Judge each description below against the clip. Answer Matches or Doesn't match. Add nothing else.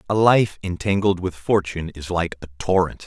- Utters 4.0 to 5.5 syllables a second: Matches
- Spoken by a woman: Doesn't match